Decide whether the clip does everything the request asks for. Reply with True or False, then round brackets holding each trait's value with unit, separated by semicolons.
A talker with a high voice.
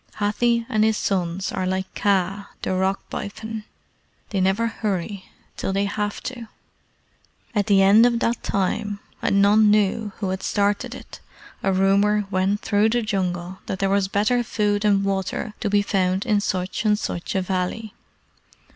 True (200 Hz)